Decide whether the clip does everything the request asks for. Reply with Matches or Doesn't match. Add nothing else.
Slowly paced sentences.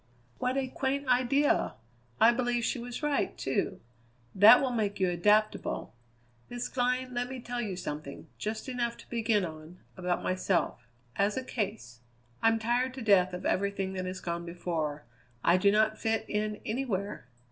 Doesn't match